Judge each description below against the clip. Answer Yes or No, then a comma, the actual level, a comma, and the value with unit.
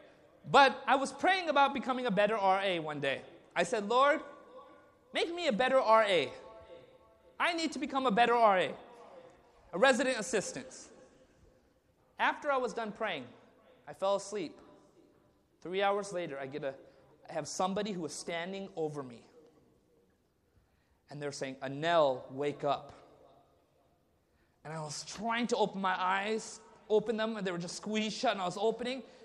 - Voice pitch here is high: Yes, high, 210 Hz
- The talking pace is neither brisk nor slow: Yes, average, 160 wpm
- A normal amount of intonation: No, wide, 8.0 semitones